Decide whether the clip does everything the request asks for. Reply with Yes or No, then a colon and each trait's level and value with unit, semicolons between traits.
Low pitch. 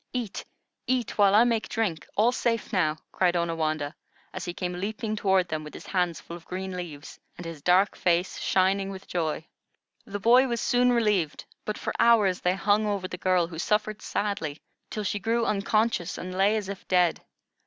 No: high, 190 Hz